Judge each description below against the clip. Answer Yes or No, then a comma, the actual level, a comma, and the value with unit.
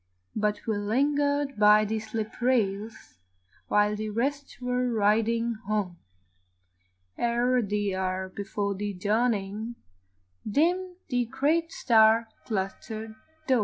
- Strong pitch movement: No, average, 3.2 semitones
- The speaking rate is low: Yes, slow, 110 wpm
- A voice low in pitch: No, high, 220 Hz